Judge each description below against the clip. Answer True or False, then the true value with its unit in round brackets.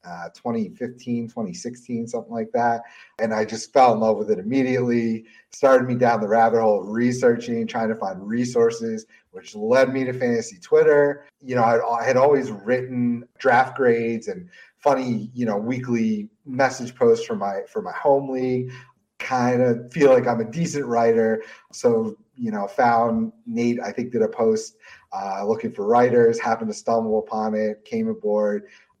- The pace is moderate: True (170 wpm)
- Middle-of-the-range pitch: False (120 Hz)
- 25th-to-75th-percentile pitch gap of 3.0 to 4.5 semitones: True (4.1 semitones)